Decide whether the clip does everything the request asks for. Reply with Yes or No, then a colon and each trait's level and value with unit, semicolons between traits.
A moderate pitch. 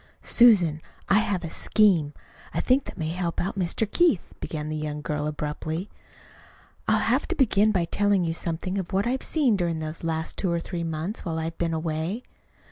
Yes: medium, 170 Hz